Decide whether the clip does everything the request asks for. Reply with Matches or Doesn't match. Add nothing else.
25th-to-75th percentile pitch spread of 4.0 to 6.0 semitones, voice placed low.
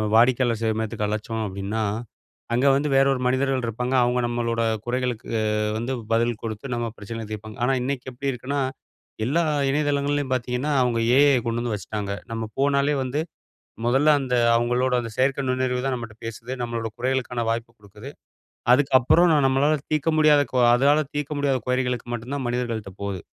Doesn't match